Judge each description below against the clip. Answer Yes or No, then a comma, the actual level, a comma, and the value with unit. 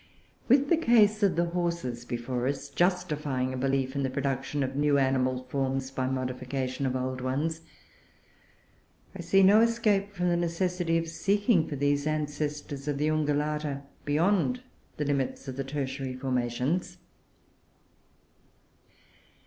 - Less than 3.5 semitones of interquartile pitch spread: No, average, 4.6 semitones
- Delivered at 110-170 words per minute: Yes, average, 140 wpm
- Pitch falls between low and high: Yes, medium, 145 Hz